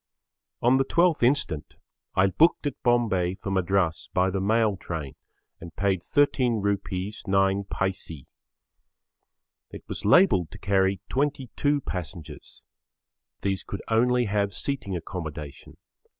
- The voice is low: Yes, low, 100 Hz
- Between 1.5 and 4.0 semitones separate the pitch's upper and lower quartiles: No, average, 5.0 semitones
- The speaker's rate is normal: No, slow, 120 wpm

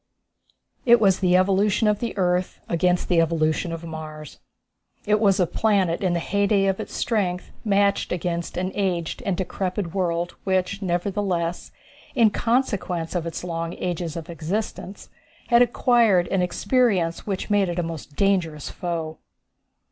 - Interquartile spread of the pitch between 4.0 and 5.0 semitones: No, average, 3.1 semitones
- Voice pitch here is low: No, medium, 180 Hz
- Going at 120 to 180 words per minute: Yes, average, 150 wpm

